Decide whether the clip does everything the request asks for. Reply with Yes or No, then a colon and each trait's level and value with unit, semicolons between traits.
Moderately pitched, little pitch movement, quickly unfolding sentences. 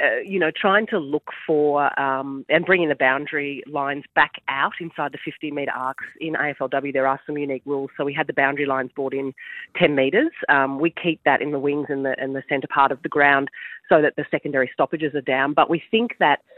Yes: medium, 145 Hz; narrow, 2.3 semitones; fast, 230 wpm